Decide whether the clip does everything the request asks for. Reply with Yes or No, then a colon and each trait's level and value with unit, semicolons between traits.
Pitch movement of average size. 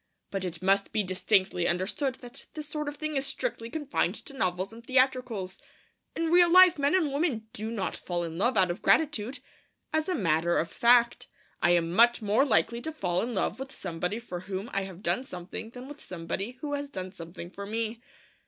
No: wide, 6.7 semitones